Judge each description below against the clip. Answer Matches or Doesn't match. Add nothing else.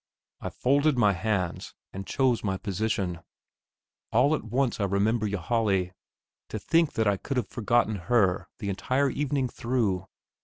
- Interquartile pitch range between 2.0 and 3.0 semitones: Doesn't match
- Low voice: Matches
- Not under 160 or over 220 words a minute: Doesn't match